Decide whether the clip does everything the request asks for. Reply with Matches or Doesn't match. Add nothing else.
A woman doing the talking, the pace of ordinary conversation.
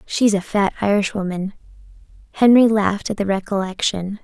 Doesn't match